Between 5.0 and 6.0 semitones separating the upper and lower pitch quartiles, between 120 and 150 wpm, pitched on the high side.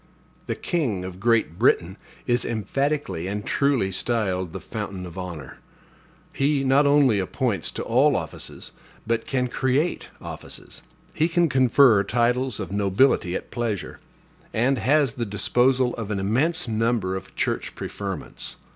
No: wide, 5.6 semitones; average, 140 wpm; low, 115 Hz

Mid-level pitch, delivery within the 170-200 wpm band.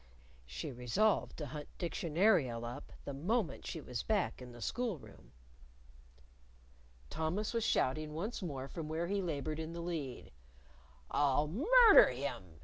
No: medium, 155 Hz; average, 145 wpm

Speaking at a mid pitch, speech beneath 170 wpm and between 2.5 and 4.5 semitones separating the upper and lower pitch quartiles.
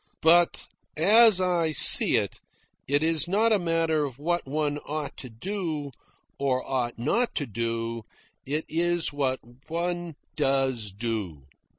No: medium, 150 Hz; slow, 135 wpm; average, 4.9 semitones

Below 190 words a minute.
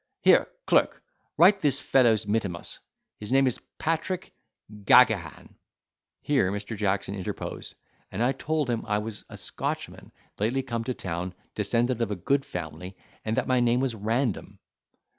Yes: average, 145 wpm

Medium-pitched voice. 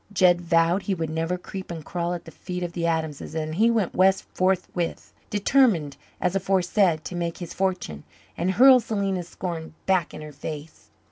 Yes: medium, 175 Hz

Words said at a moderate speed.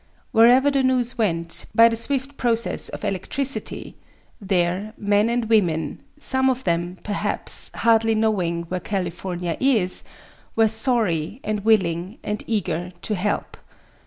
No: slow, 130 wpm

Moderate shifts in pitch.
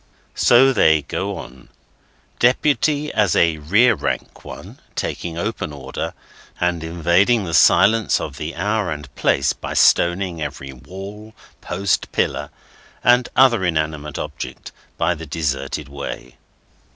No: wide, 5.9 semitones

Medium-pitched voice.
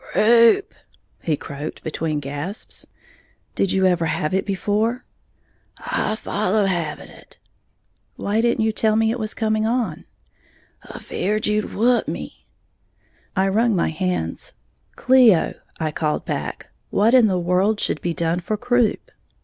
No: high, 205 Hz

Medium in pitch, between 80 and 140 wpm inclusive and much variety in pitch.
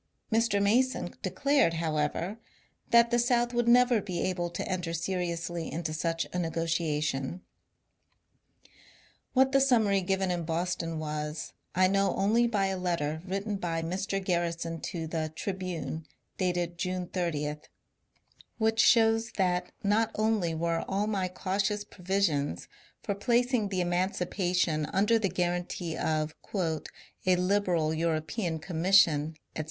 No: medium, 180 Hz; slow, 135 wpm; average, 3.6 semitones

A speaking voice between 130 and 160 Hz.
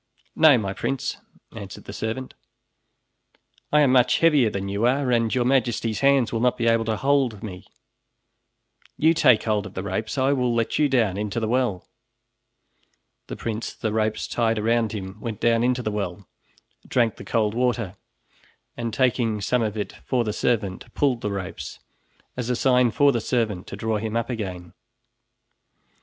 No: low, 115 Hz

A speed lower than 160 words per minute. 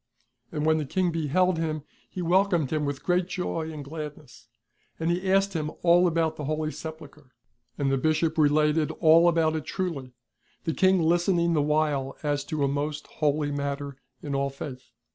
No: average, 180 wpm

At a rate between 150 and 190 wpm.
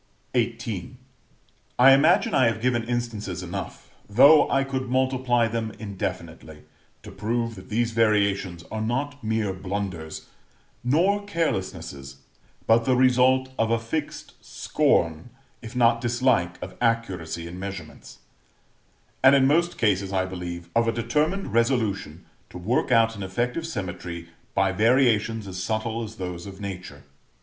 No: average, 140 wpm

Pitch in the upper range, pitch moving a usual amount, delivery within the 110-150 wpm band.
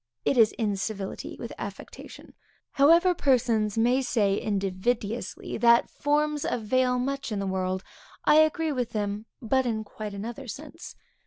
Yes: high, 235 Hz; average, 4.6 semitones; average, 140 wpm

